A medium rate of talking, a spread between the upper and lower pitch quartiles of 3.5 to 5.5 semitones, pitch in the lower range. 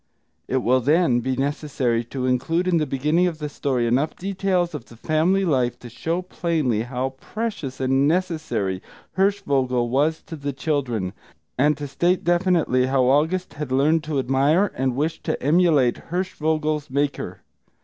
No: average, 160 wpm; average, 4.4 semitones; medium, 145 Hz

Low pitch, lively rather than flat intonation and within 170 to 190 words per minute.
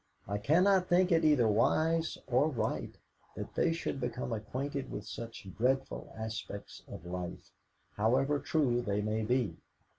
No: low, 125 Hz; wide, 5.9 semitones; average, 145 wpm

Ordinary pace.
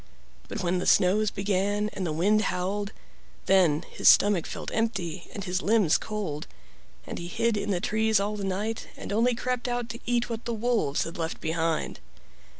Yes: average, 180 wpm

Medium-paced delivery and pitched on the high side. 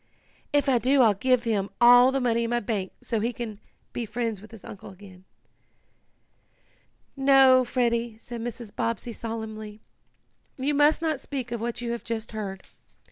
Yes: average, 170 wpm; high, 235 Hz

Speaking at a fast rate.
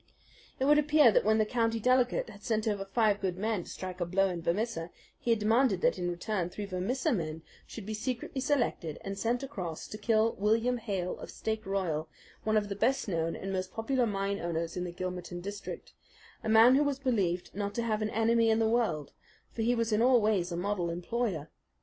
Yes: fast, 215 wpm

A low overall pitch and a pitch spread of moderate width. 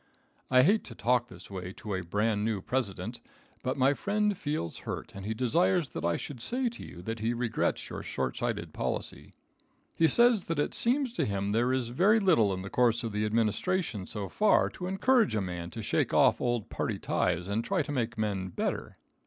No: low, 115 Hz; wide, 8.4 semitones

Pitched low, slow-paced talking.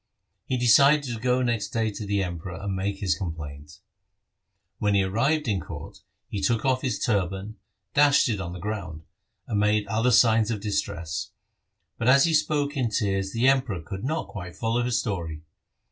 No: low, 105 Hz; average, 180 wpm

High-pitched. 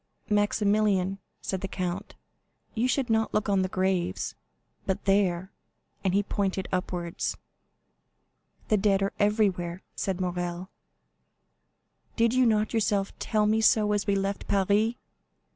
Yes: high, 200 Hz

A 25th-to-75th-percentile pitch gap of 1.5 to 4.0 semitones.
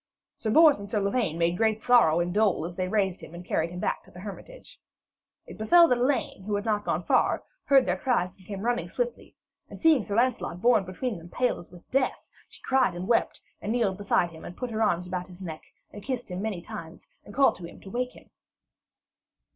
No: wide, 5.5 semitones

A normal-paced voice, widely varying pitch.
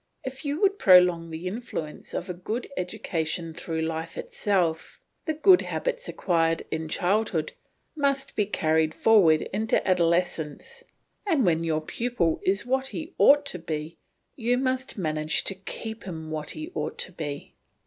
Yes: average, 155 wpm; wide, 7.5 semitones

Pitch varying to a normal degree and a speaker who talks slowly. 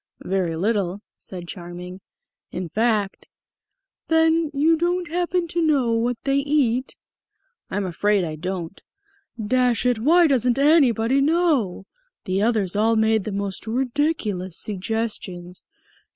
No: wide, 6.6 semitones; slow, 125 wpm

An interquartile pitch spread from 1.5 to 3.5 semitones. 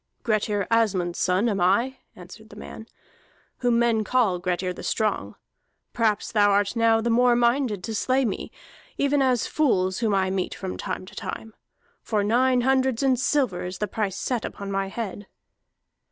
No: average, 3.9 semitones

